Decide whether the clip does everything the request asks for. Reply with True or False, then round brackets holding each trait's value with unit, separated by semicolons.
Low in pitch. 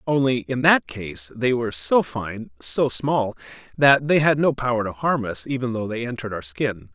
True (120 Hz)